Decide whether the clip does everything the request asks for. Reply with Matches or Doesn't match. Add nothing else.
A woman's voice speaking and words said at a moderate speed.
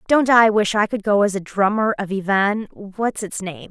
Doesn't match